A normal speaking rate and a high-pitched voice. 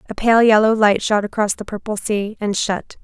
No: fast, 215 wpm; high, 210 Hz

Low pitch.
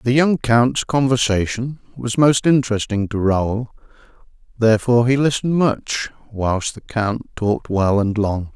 Yes: low, 115 Hz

